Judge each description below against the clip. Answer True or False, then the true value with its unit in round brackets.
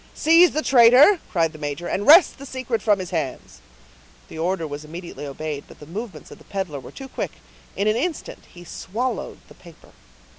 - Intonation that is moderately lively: False (8.3 semitones)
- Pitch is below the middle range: False (190 Hz)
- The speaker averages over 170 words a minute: True (195 wpm)